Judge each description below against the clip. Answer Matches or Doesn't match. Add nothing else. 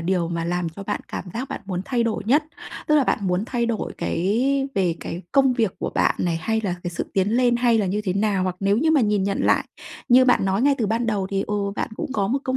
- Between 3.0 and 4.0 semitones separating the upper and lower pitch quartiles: Doesn't match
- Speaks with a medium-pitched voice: Doesn't match